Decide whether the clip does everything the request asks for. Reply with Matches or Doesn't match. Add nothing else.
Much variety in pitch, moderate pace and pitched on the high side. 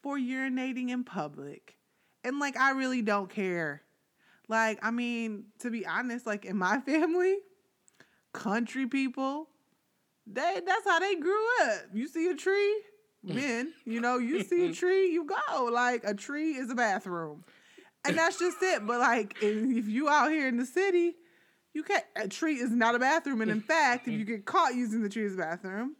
Matches